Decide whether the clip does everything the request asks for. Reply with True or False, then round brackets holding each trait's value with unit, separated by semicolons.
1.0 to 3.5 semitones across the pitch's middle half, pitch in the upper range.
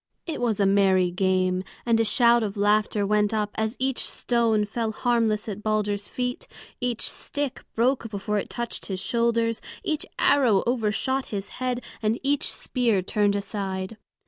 True (2.8 semitones; 220 Hz)